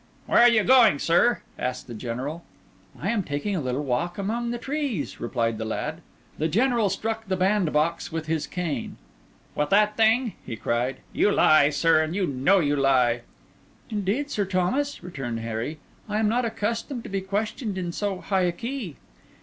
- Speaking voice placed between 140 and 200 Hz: Yes, medium, 185 Hz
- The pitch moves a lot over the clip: Yes, wide, 7.3 semitones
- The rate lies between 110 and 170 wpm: No, average, 180 wpm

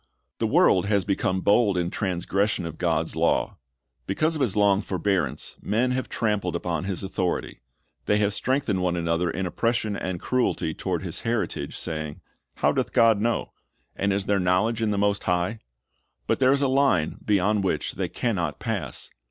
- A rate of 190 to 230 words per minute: No, average, 180 wpm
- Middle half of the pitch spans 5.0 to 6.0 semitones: No, average, 3.7 semitones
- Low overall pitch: Yes, low, 100 Hz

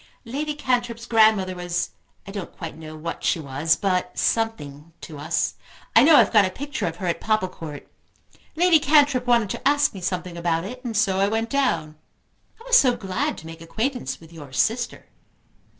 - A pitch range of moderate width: No, wide, 6.8 semitones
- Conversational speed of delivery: Yes, average, 185 wpm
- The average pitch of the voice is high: Yes, high, 195 Hz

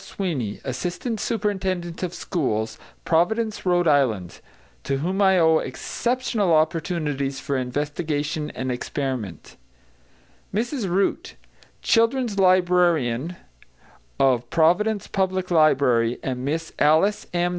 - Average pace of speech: No, slow, 100 wpm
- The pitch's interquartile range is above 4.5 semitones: Yes, wide, 5.5 semitones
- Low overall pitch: No, medium, 165 Hz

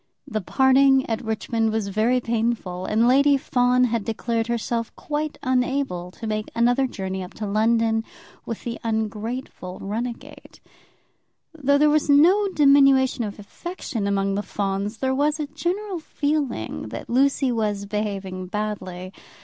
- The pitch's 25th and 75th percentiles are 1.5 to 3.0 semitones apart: No, average, 4.6 semitones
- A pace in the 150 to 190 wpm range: No, average, 140 wpm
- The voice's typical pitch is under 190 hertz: No, high, 230 Hz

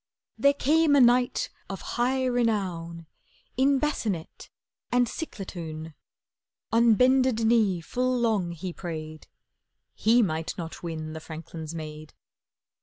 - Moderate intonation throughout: No, wide, 7.2 semitones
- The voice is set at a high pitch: Yes, high, 205 Hz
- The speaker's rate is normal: No, slow, 115 wpm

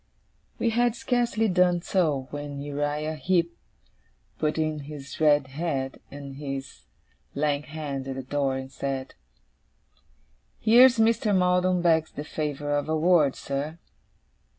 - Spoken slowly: Yes, slow, 130 wpm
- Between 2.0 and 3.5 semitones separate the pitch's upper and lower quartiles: No, average, 4.2 semitones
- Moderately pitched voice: Yes, medium, 150 Hz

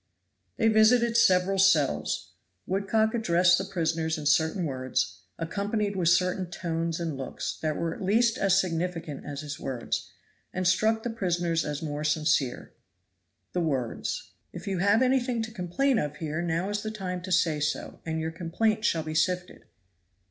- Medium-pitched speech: Yes, medium, 175 Hz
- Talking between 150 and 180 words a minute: Yes, average, 165 wpm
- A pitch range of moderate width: Yes, average, 4.2 semitones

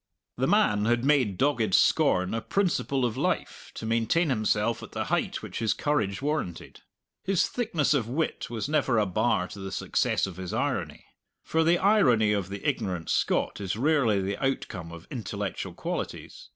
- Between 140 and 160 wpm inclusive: No, average, 175 wpm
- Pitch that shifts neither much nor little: No, wide, 6.6 semitones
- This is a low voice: Yes, low, 115 Hz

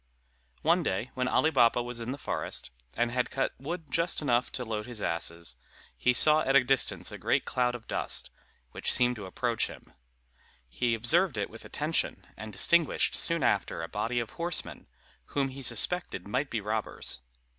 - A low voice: Yes, low, 125 Hz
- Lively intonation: No, average, 3.7 semitones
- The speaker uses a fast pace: No, average, 180 wpm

